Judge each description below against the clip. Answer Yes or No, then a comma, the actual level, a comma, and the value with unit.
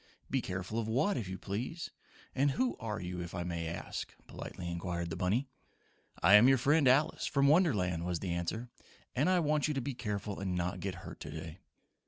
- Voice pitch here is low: Yes, low, 105 Hz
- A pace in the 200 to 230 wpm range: Yes, fast, 205 wpm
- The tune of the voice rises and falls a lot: Yes, wide, 7.5 semitones